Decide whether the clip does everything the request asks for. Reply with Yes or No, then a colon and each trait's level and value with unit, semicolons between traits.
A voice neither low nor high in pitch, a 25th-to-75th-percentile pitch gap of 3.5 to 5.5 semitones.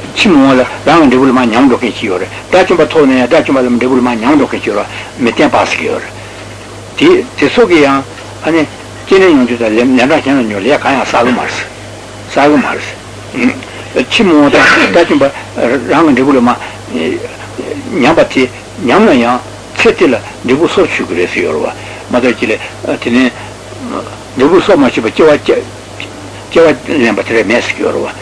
No: low, 125 Hz; average, 4.1 semitones